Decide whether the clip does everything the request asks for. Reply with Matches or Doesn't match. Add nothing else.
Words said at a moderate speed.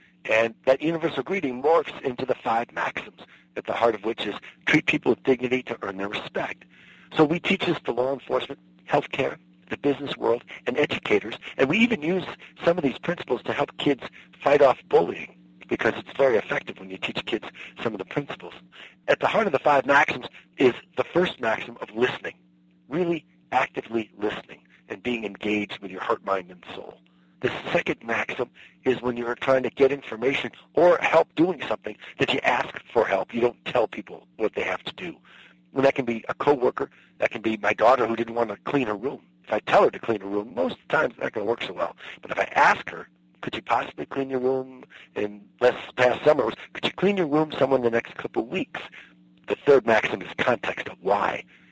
Doesn't match